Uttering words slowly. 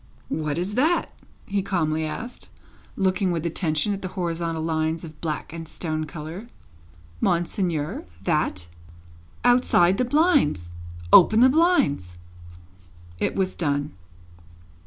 Yes: slow, 115 wpm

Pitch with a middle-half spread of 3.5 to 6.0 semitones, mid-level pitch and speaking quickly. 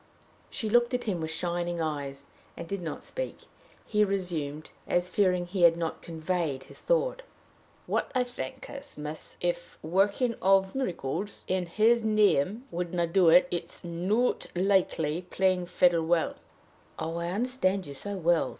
No: average, 3.8 semitones; medium, 180 Hz; average, 170 wpm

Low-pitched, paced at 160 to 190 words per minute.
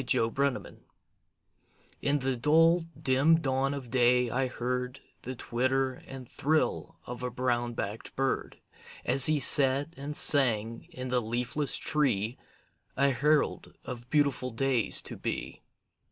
No: low, 130 Hz; average, 140 wpm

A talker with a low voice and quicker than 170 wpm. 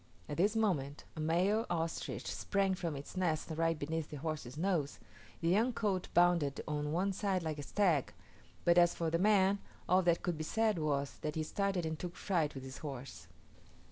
No: medium, 165 Hz; average, 195 wpm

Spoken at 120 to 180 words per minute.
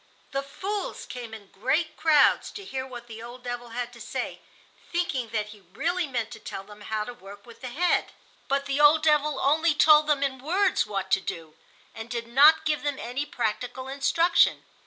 No: average, 200 wpm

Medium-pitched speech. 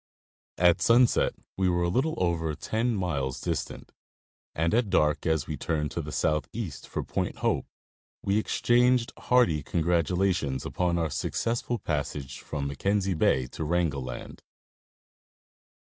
No: very low, 85 Hz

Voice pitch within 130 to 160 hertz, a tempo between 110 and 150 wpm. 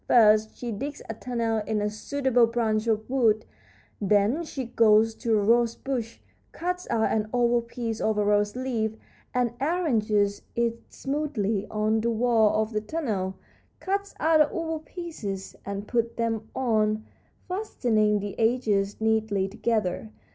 No: high, 225 Hz; average, 145 wpm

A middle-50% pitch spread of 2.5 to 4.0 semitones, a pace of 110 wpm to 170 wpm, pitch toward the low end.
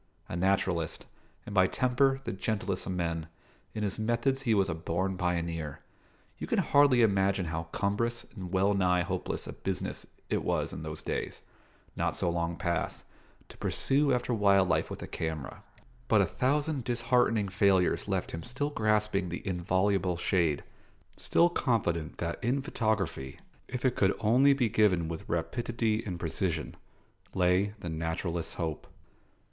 No: average, 5.2 semitones; average, 155 wpm; very low, 95 Hz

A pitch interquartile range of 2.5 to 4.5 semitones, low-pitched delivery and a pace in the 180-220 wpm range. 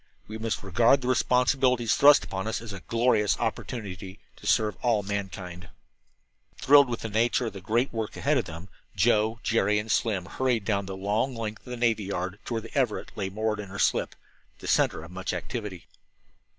Yes: average, 3.4 semitones; low, 110 Hz; average, 200 wpm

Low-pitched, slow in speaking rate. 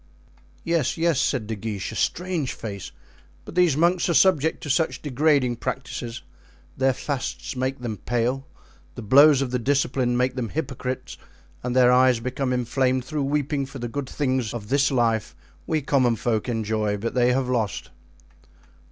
No: low, 130 Hz; average, 165 wpm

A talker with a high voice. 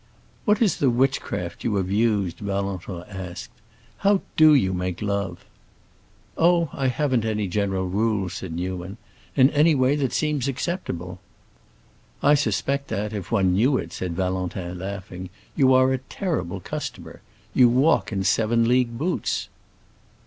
No: low, 110 Hz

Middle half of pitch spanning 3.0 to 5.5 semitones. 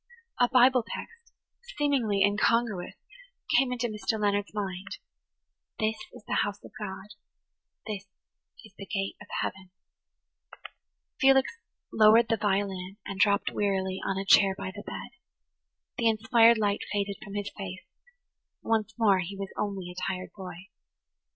No: narrow, 2.6 semitones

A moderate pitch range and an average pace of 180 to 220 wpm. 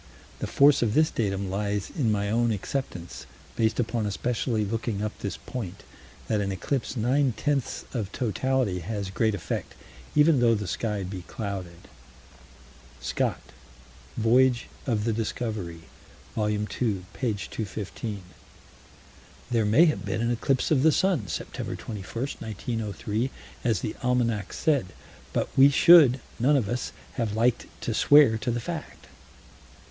No: average, 3.7 semitones; average, 140 wpm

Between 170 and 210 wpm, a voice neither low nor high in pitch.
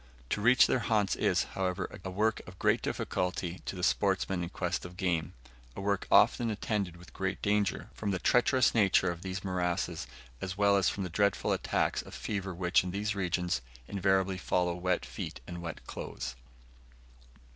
No: average, 180 wpm; very low, 95 Hz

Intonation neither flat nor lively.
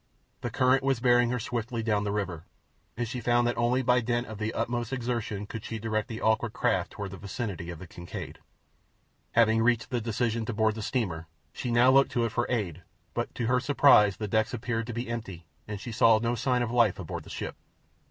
No: narrow, 2.3 semitones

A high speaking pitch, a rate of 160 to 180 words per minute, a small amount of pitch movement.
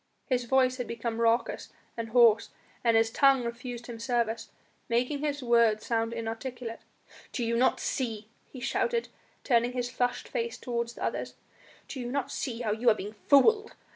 Yes: high, 240 Hz; average, 170 wpm; narrow, 1.9 semitones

